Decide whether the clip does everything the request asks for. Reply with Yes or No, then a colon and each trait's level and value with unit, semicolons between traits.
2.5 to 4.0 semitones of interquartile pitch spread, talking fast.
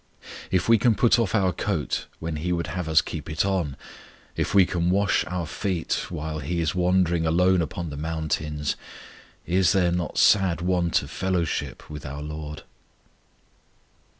No: average, 3.1 semitones; average, 165 wpm